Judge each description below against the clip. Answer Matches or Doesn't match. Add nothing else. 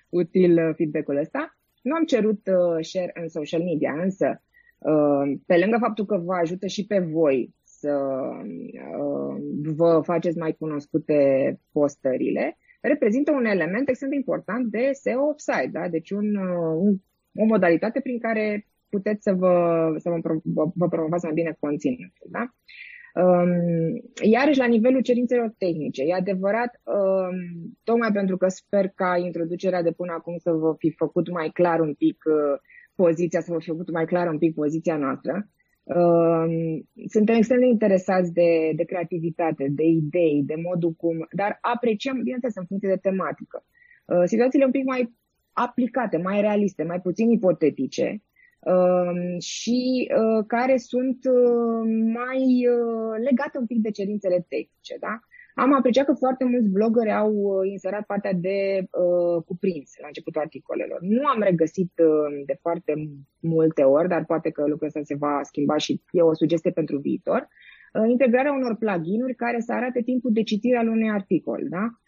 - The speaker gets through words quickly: Doesn't match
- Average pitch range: Doesn't match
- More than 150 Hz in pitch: Matches